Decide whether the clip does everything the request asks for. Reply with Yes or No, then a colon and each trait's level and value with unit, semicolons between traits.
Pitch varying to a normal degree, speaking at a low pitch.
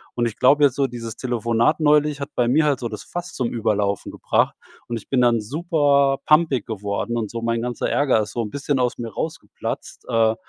Yes: average, 3.8 semitones; low, 120 Hz